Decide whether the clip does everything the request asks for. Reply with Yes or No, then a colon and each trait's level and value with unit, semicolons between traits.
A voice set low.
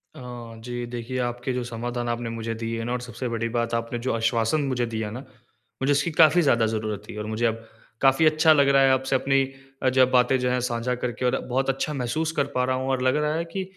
Yes: low, 125 Hz